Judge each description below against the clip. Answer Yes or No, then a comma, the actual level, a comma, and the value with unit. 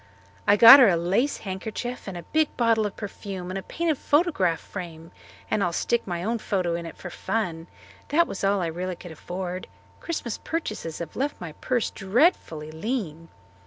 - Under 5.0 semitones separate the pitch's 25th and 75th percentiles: No, wide, 5.5 semitones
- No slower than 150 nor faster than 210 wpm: Yes, average, 185 wpm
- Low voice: No, high, 195 Hz